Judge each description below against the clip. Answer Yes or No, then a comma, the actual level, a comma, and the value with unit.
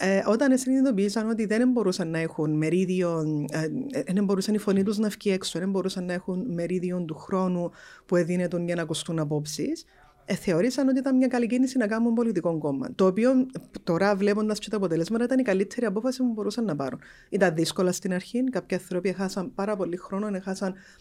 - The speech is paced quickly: Yes, fast, 190 wpm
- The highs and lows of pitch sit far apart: No, average, 4.4 semitones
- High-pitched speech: Yes, high, 195 Hz